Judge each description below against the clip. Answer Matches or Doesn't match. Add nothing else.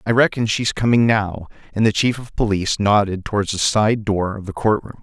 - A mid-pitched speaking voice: Doesn't match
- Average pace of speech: Doesn't match